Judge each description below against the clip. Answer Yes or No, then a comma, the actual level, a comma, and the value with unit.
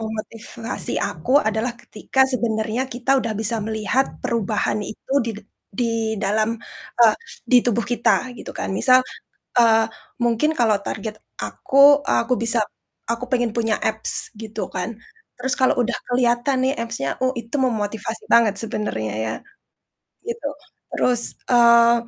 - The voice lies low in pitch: No, high, 230 Hz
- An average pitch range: No, narrow, 2.3 semitones